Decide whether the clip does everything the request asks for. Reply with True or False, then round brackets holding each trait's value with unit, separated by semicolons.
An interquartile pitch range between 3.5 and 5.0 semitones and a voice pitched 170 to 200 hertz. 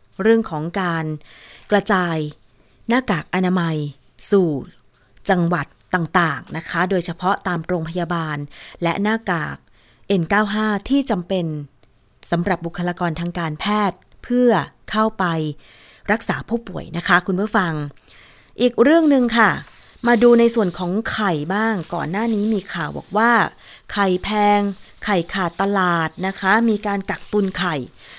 True (3.9 semitones; 185 Hz)